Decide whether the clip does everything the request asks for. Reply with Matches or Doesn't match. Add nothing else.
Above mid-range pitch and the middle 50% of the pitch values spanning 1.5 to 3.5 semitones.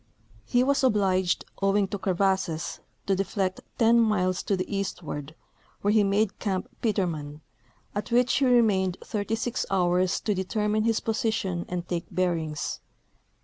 Matches